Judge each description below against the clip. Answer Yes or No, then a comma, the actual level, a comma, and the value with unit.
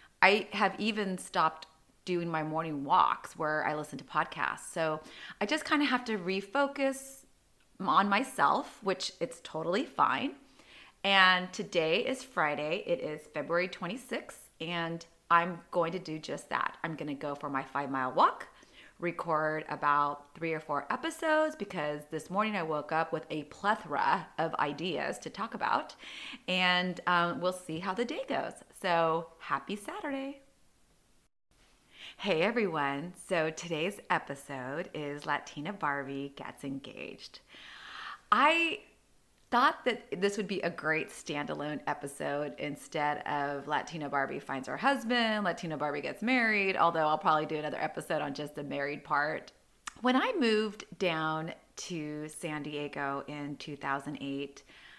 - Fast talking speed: No, average, 145 wpm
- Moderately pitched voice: Yes, medium, 165 Hz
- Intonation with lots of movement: Yes, wide, 5.8 semitones